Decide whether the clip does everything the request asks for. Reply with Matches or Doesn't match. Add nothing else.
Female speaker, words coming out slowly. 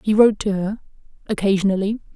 Matches